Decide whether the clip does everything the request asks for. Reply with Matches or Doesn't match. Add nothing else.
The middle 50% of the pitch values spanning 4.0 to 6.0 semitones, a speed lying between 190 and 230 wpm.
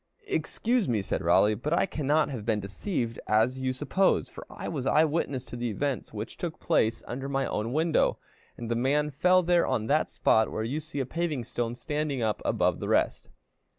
Matches